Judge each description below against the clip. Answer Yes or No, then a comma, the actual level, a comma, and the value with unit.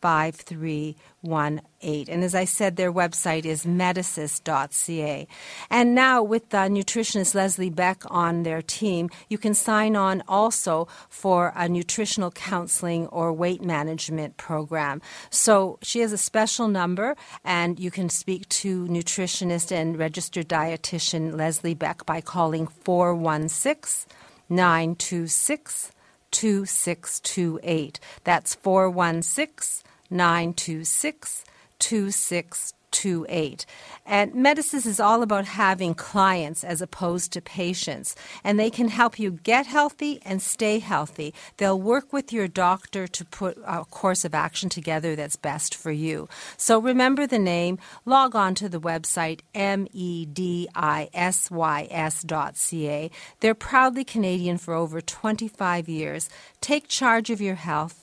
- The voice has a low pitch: No, medium, 180 Hz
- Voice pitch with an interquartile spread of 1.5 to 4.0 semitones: Yes, average, 3.7 semitones